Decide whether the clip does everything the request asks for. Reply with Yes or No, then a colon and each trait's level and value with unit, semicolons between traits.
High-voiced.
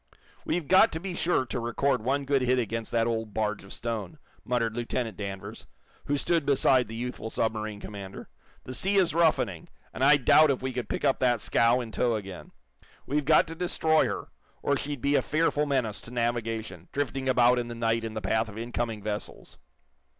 No: low, 120 Hz